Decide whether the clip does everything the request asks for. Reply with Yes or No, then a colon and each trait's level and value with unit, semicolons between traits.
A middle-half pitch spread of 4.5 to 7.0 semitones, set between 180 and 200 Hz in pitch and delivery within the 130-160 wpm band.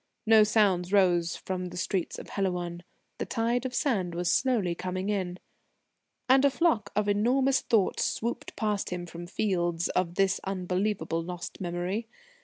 No: average, 3.6 semitones; high, 190 Hz; average, 155 wpm